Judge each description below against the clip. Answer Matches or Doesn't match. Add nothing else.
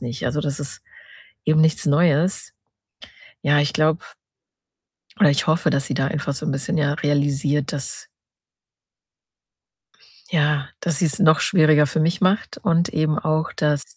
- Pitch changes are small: Matches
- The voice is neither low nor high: Matches